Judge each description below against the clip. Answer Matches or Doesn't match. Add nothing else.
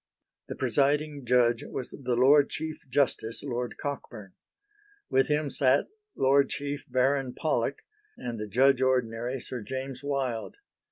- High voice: Doesn't match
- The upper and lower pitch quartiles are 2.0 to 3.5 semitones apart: Matches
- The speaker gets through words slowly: Matches